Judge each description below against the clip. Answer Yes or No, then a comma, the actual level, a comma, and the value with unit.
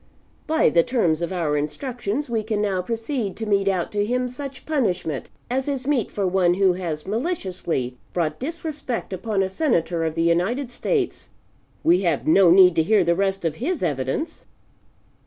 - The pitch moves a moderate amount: No, wide, 6.5 semitones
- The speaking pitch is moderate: No, high, 195 Hz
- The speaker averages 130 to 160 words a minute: No, average, 175 wpm